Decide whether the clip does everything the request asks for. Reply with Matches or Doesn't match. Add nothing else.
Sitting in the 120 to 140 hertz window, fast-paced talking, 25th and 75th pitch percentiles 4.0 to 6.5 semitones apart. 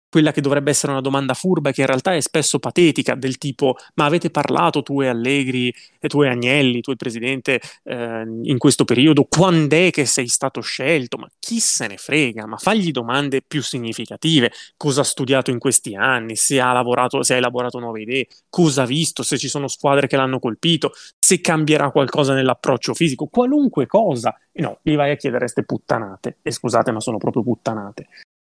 Doesn't match